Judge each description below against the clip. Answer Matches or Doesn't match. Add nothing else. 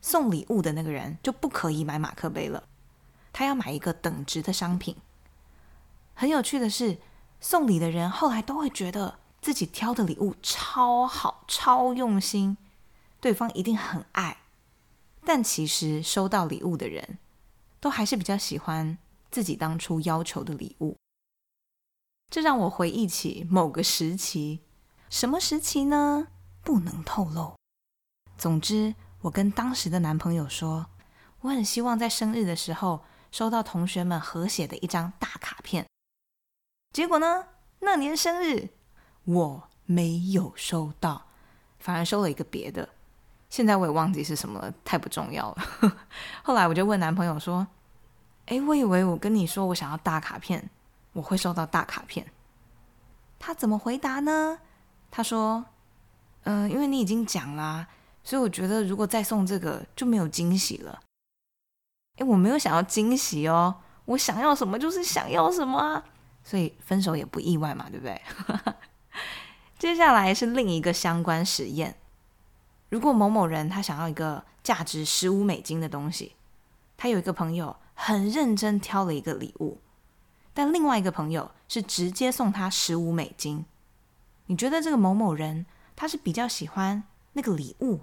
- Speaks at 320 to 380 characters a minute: Doesn't match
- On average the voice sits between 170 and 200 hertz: Matches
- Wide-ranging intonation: Matches